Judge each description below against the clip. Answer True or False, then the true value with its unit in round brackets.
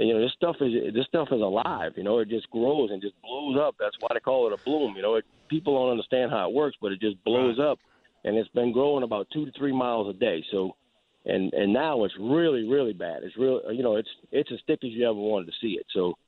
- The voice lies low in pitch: True (125 Hz)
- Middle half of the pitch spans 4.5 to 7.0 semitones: True (5.1 semitones)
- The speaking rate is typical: False (275 wpm)